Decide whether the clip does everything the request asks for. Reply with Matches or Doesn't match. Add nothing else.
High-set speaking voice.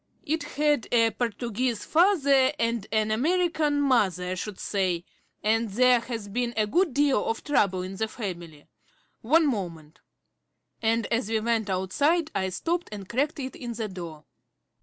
Matches